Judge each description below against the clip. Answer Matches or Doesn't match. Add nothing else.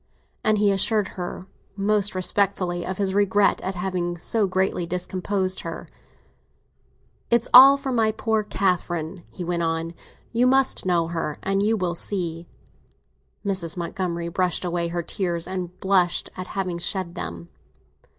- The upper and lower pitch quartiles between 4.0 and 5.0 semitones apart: Doesn't match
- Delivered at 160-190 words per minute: Doesn't match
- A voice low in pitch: Doesn't match